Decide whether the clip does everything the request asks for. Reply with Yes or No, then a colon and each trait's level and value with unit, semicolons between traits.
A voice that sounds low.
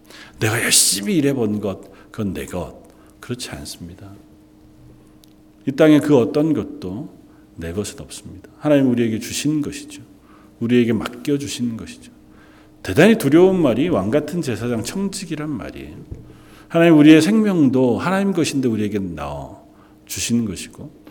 Yes: low, 120 Hz